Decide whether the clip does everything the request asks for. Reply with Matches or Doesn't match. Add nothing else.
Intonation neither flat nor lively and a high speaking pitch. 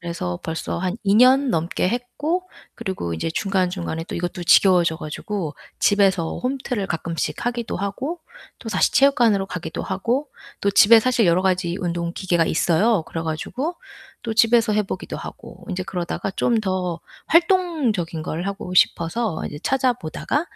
Doesn't match